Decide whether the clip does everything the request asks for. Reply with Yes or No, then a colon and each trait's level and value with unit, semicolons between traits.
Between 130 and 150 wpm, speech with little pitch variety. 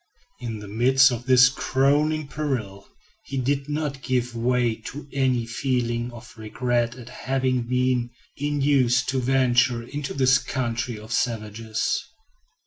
Yes: slow, 135 wpm; narrow, 2.3 semitones